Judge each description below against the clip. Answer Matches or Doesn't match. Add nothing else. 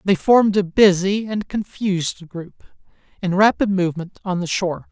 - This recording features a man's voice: Matches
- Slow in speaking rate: Doesn't match